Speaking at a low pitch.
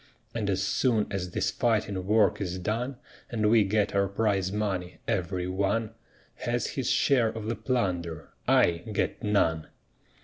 Yes: low, 100 Hz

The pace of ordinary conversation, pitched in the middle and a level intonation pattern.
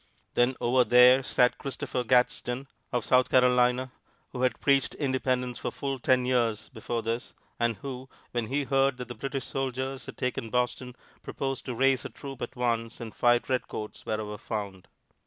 No: average, 170 wpm; low, 125 Hz; narrow, 1.6 semitones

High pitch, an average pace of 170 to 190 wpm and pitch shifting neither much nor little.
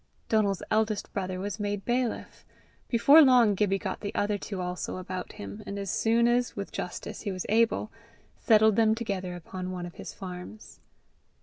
Yes: high, 205 Hz; average, 175 wpm; average, 3.2 semitones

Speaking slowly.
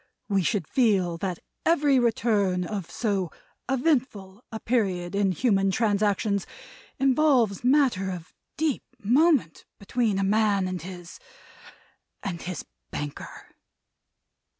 Yes: slow, 110 wpm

